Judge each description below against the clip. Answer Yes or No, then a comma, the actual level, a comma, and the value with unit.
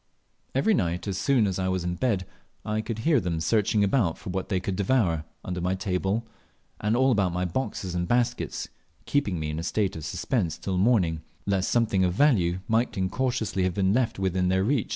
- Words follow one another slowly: No, fast, 205 wpm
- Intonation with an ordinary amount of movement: Yes, average, 4.1 semitones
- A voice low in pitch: Yes, very low, 95 Hz